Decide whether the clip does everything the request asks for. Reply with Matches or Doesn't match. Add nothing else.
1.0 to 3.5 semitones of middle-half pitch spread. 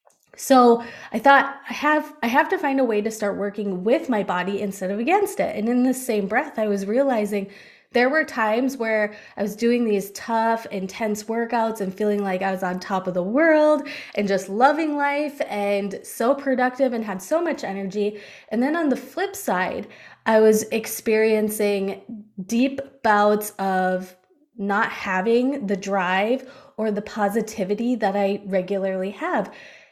Doesn't match